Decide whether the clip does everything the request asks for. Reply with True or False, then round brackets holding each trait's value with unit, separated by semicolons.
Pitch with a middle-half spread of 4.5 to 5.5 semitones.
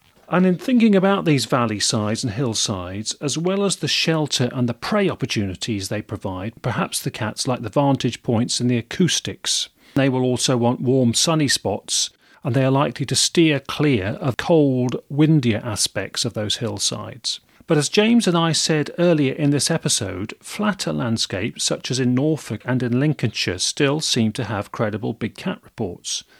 True (5.1 semitones)